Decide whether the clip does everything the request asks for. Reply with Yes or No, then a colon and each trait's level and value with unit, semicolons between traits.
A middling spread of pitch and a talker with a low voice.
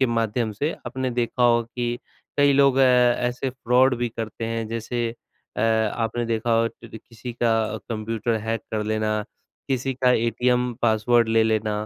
No: narrow, 1.7 semitones; low, 115 Hz